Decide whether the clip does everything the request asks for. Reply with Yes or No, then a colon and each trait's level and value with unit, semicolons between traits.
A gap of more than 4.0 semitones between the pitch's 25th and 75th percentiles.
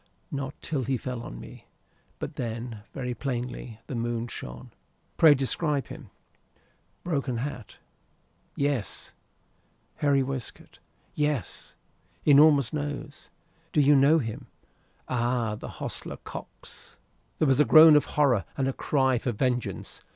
No: average, 3.3 semitones